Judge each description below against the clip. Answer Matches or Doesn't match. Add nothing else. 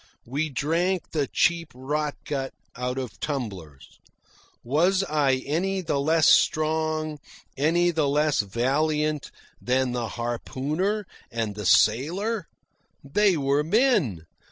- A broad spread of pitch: Doesn't match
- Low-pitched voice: Doesn't match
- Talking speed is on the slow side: Matches